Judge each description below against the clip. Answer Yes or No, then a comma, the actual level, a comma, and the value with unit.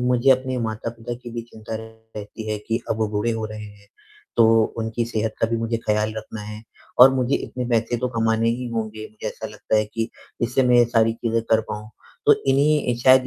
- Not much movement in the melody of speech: Yes, narrow, 1.8 semitones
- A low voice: Yes, low, 115 Hz